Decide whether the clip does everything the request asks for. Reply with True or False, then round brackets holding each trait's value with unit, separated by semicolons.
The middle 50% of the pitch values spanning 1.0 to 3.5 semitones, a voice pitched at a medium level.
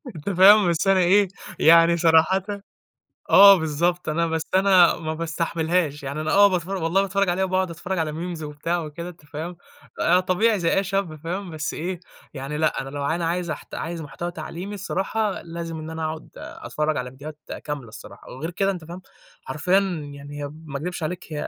True (2.9 semitones; 170 Hz)